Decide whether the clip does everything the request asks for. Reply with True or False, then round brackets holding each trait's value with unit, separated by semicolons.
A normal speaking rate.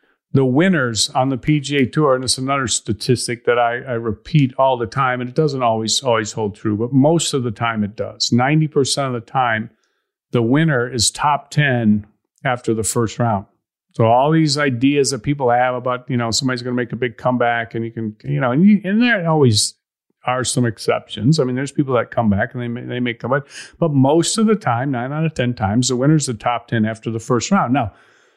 False (230 wpm)